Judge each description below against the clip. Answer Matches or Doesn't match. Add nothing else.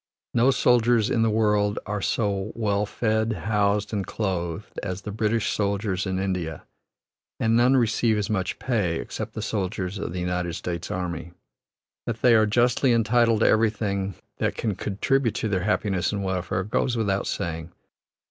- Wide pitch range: Doesn't match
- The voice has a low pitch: Matches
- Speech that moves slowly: Doesn't match